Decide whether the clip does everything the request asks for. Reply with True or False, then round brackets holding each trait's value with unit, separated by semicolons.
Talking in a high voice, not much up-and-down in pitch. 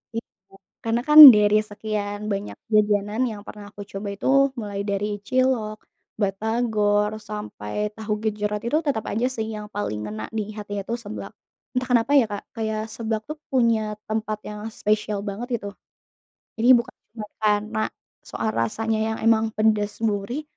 True (215 Hz; 1.4 semitones)